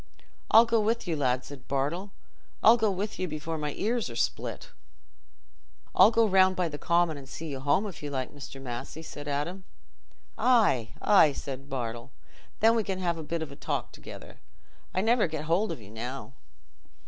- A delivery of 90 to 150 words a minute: No, average, 185 wpm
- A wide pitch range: Yes, wide, 6.5 semitones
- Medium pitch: Yes, medium, 160 Hz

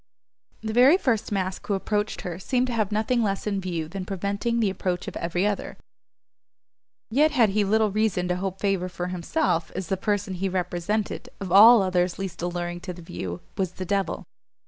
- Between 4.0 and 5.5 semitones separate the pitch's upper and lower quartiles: No, average, 3.0 semitones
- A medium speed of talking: Yes, average, 190 wpm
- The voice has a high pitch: Yes, high, 195 Hz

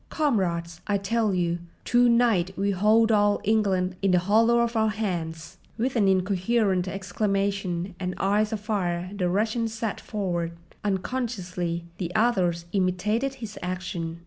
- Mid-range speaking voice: No, high, 195 Hz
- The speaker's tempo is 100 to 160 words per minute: Yes, average, 140 wpm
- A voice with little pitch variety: No, average, 3.4 semitones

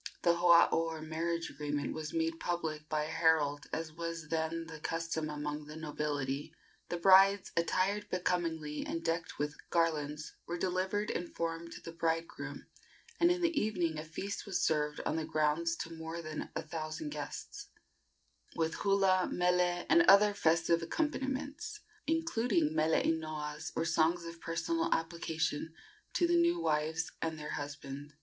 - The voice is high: No, medium, 165 Hz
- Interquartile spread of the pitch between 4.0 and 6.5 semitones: No, narrow, 2.5 semitones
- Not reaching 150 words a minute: No, average, 155 wpm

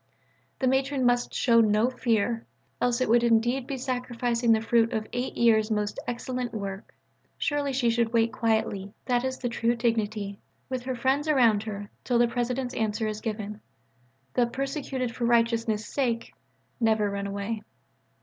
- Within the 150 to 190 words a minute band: Yes, average, 160 wpm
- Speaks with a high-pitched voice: Yes, high, 235 Hz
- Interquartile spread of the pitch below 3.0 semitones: Yes, narrow, 2.4 semitones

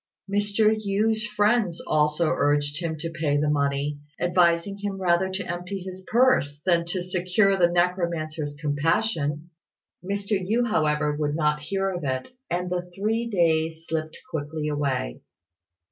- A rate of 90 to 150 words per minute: Yes, average, 145 wpm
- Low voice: No, medium, 175 Hz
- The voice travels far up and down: No, average, 4.5 semitones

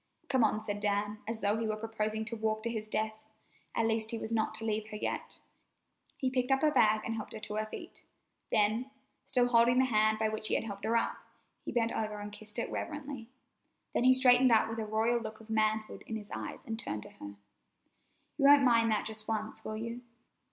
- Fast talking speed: Yes, fast, 230 wpm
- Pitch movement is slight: Yes, narrow, 1.4 semitones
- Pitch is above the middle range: Yes, high, 220 Hz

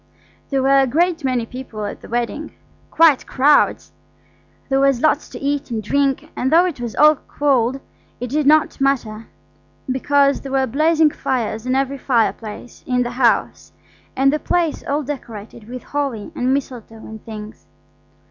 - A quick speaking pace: No, average, 160 wpm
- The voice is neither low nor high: No, very high, 265 Hz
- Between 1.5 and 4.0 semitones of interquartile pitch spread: Yes, average, 3.2 semitones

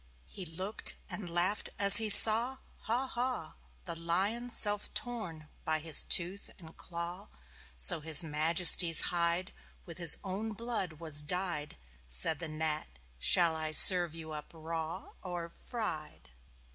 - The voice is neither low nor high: Yes, medium, 175 Hz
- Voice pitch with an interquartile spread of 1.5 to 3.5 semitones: No, average, 4.0 semitones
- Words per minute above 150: No, average, 140 wpm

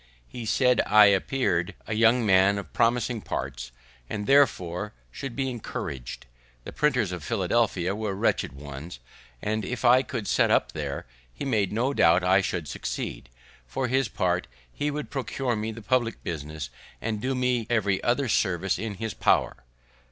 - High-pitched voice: No, low, 110 Hz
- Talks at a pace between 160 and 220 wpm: Yes, average, 165 wpm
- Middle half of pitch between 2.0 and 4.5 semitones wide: No, average, 5.2 semitones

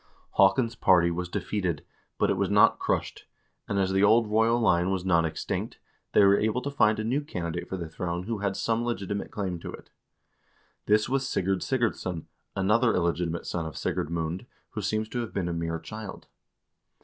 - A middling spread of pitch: Yes, average, 4.0 semitones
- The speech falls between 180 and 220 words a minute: Yes, average, 190 wpm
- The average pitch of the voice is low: Yes, low, 100 Hz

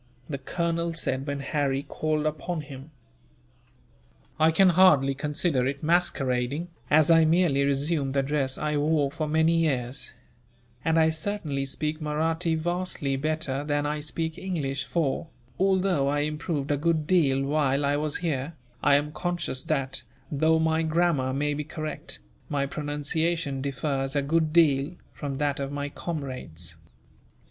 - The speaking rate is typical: Yes, average, 150 wpm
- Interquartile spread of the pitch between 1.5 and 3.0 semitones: Yes, average, 2.7 semitones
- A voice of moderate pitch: Yes, medium, 150 Hz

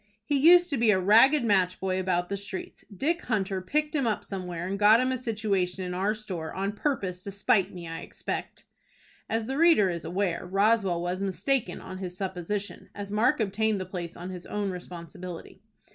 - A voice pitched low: No, high, 195 Hz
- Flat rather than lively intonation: No, average, 3.3 semitones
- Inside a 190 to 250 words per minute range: Yes, average, 195 wpm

